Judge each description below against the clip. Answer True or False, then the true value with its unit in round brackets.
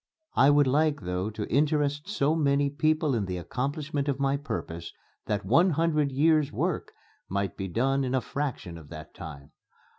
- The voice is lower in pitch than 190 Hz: True (140 Hz)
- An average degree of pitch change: False (6.3 semitones)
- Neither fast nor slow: True (175 wpm)